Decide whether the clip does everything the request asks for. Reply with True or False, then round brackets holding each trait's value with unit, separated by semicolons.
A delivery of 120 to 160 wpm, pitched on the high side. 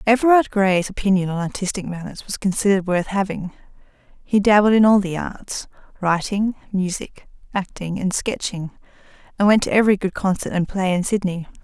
True (155 wpm; 195 Hz)